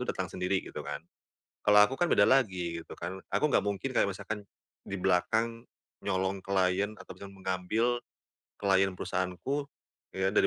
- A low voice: Yes, low, 100 Hz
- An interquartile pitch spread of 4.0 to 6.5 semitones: No, narrow, 2.6 semitones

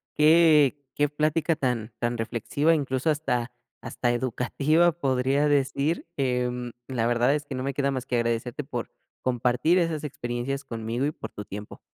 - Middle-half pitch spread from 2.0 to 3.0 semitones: No, average, 3.4 semitones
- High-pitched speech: No, low, 130 Hz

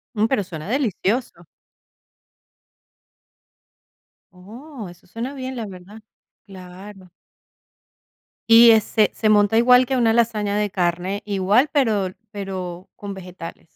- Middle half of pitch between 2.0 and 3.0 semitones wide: No, average, 3.8 semitones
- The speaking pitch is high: Yes, high, 205 Hz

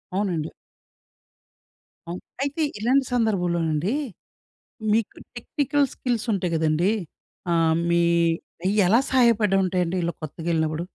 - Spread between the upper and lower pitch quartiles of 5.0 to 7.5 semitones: Yes, wide, 5.4 semitones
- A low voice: No, medium, 185 Hz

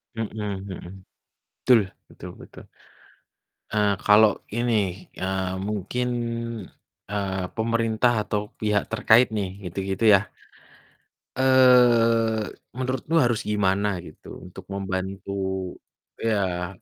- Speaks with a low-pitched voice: Yes, low, 105 Hz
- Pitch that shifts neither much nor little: Yes, average, 3.2 semitones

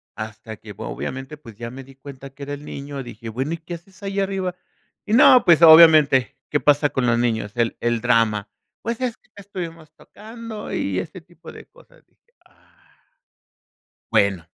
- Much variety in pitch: Yes, wide, 7.6 semitones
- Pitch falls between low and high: Yes, medium, 145 Hz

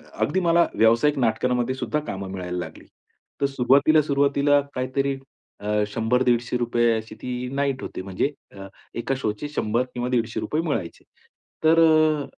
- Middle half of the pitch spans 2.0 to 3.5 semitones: No, average, 4.0 semitones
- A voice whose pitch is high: No, low, 125 Hz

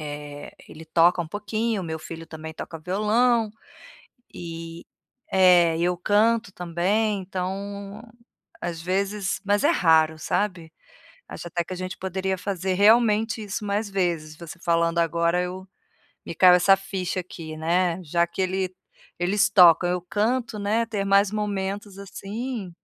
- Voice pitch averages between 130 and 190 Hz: Yes, medium, 185 Hz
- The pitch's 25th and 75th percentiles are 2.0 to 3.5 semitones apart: Yes, average, 3.2 semitones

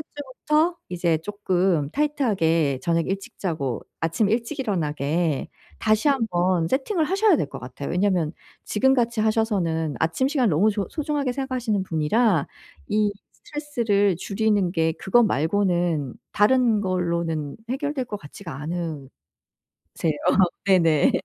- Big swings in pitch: Yes, wide, 6.6 semitones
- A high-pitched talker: Yes, high, 195 Hz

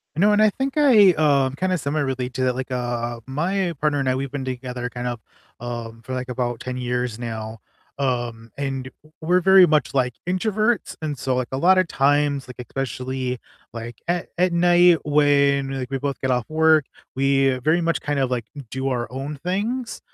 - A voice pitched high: No, low, 135 Hz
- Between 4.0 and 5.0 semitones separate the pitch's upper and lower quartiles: Yes, average, 4.6 semitones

